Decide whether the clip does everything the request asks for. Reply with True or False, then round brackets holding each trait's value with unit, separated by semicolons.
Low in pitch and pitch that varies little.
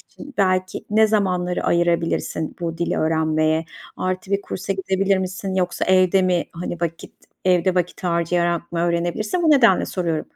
False (180 Hz; 2.0 semitones)